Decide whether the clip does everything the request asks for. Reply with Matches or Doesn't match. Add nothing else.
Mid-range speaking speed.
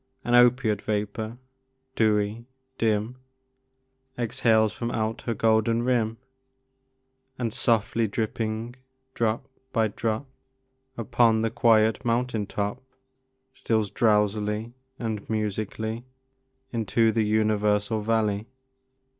Doesn't match